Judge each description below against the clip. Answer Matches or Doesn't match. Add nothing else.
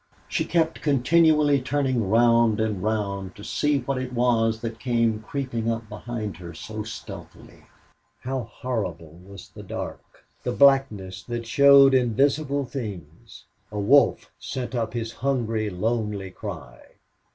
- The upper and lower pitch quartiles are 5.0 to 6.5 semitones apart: Doesn't match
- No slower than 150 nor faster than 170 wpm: Doesn't match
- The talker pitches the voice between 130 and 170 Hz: Doesn't match